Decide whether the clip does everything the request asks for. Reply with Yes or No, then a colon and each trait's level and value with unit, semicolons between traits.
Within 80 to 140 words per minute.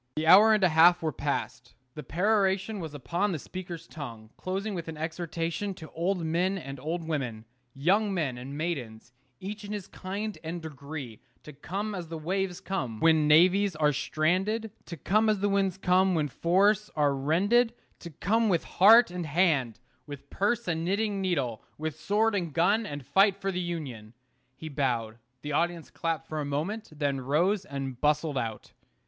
No: average, 180 wpm